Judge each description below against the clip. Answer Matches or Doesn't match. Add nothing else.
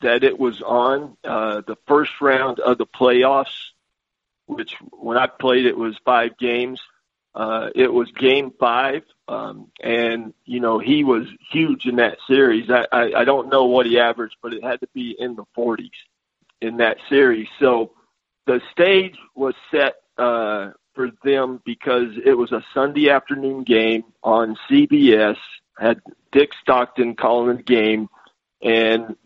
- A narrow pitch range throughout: Doesn't match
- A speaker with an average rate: Matches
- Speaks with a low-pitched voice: Matches